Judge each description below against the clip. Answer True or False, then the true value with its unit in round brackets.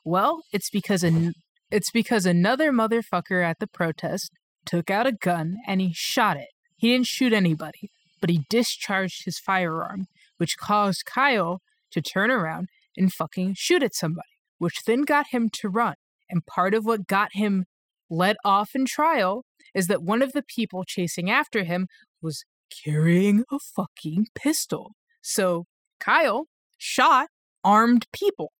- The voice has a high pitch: True (195 Hz)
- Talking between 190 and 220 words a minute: False (155 wpm)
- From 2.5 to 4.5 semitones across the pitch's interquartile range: False (5.2 semitones)